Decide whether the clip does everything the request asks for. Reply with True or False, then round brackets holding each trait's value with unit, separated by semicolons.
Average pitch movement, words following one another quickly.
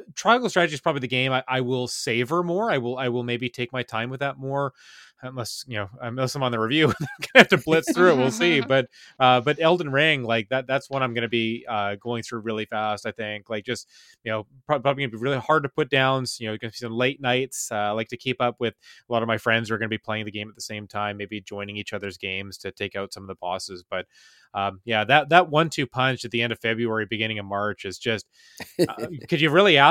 True (3.9 semitones; 275 wpm)